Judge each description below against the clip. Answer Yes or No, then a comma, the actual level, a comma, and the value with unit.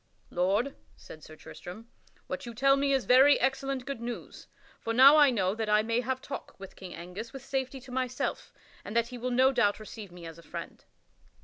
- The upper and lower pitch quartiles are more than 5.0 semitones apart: No, average, 4.3 semitones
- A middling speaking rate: No, fast, 210 wpm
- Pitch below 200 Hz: No, high, 240 Hz